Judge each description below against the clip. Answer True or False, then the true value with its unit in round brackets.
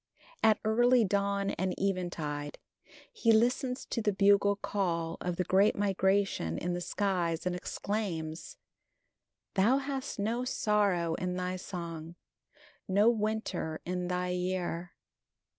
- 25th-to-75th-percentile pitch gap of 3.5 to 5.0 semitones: False (3.0 semitones)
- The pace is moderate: False (125 wpm)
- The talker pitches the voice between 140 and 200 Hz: True (190 Hz)